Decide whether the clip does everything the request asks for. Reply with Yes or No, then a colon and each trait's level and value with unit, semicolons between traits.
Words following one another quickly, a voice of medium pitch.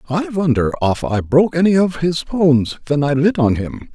Yes: fast, 215 wpm; medium, 150 Hz